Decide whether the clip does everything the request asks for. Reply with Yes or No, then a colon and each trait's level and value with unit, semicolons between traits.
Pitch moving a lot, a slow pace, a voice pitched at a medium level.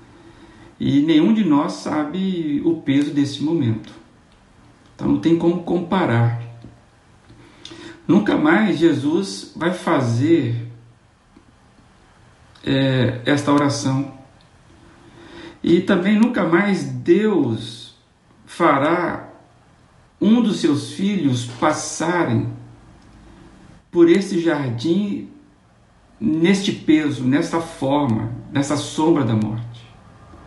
Yes: wide, 6.4 semitones; slow, 85 wpm; medium, 145 Hz